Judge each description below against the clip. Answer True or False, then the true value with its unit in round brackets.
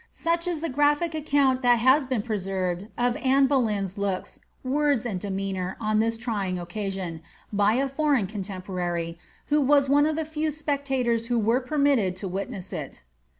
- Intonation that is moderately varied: False (6.5 semitones)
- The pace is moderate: True (170 wpm)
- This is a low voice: False (235 Hz)